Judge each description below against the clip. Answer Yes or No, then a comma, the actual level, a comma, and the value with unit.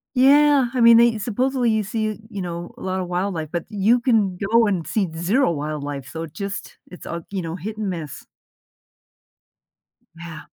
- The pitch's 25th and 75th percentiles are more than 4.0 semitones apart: Yes, average, 5.3 semitones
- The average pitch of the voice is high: Yes, high, 195 Hz